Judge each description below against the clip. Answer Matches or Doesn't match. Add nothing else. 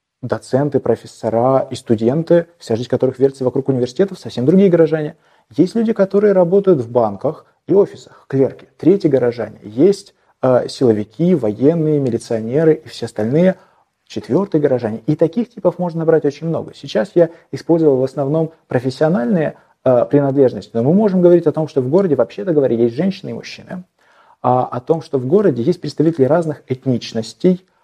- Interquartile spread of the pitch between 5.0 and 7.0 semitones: Matches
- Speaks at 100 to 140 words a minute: Doesn't match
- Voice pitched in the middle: Matches